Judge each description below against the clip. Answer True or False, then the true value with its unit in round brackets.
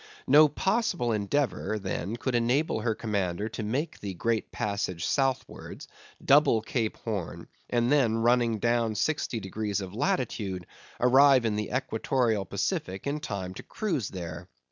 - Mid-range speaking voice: False (115 Hz)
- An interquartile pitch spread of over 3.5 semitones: True (4.5 semitones)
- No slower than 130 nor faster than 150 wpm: True (145 wpm)